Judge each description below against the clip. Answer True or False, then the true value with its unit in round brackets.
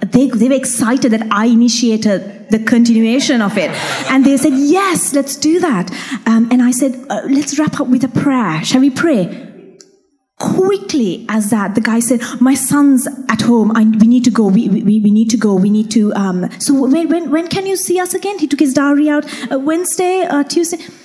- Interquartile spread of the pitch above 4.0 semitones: True (4.6 semitones)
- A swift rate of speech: True (220 wpm)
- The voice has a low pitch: False (255 Hz)